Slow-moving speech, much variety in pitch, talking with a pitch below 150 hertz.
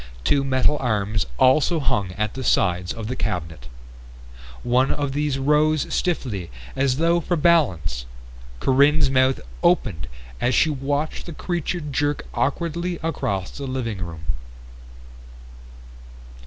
Yes: slow, 125 wpm; wide, 5.9 semitones; low, 135 Hz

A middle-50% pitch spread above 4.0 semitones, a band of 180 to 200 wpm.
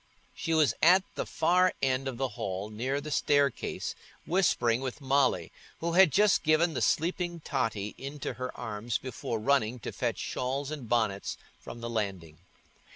No: average, 5.3 semitones; average, 160 wpm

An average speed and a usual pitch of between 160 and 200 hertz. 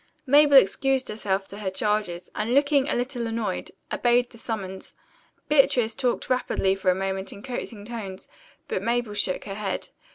No: average, 165 wpm; high, 220 Hz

